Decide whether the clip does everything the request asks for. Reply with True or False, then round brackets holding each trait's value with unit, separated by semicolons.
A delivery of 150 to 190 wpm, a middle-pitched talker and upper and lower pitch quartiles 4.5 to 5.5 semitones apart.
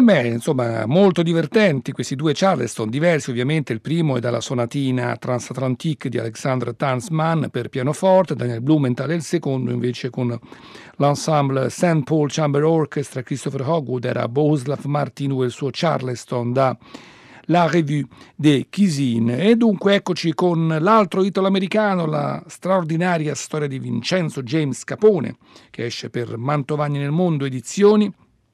False (135 wpm; 145 Hz; 4.9 semitones)